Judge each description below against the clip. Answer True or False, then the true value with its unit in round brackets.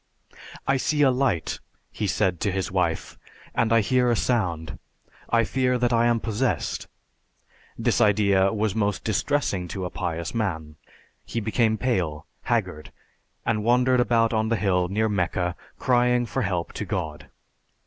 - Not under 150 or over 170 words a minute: True (155 wpm)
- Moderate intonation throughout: True (4.6 semitones)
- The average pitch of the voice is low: True (110 Hz)